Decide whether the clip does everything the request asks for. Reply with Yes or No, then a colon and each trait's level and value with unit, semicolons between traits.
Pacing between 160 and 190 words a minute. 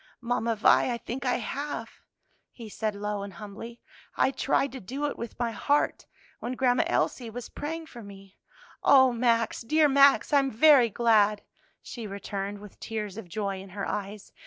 Yes: average, 180 wpm